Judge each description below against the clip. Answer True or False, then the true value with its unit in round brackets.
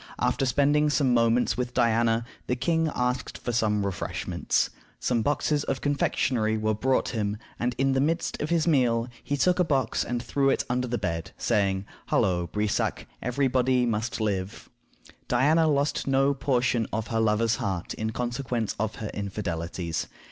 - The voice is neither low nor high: False (120 Hz)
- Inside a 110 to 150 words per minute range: False (165 wpm)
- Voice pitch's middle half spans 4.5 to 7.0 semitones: False (4.0 semitones)